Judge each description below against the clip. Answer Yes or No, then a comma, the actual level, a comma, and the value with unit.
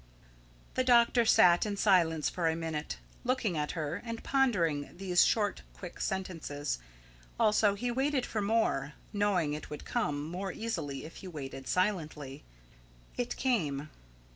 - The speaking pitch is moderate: Yes, medium, 180 Hz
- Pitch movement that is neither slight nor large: No, wide, 6.6 semitones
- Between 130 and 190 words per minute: Yes, average, 140 wpm